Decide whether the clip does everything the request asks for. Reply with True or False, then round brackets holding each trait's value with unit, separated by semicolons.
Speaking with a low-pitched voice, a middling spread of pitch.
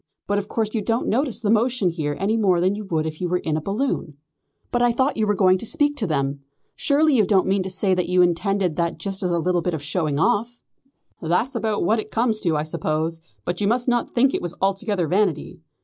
False (195 Hz; 4.6 semitones)